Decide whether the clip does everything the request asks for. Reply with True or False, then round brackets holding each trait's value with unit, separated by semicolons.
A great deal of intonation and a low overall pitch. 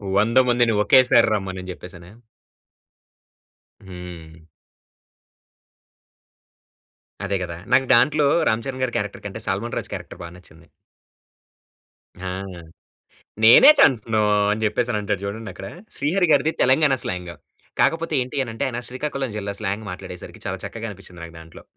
True (5.7 semitones; 110 Hz)